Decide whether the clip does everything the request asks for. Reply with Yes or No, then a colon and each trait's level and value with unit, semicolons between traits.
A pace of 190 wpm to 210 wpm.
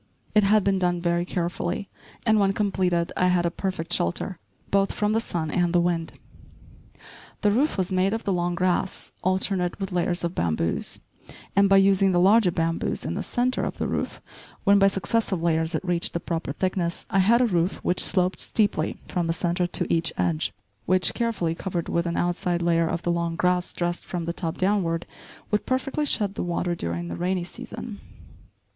Yes: average, 195 wpm